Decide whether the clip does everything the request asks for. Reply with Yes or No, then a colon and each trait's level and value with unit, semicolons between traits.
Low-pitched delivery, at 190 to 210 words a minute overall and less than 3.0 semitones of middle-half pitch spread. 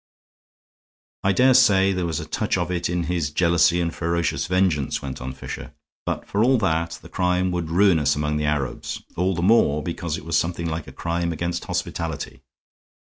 Yes: very low, 85 Hz; average, 195 wpm; narrow, 2.4 semitones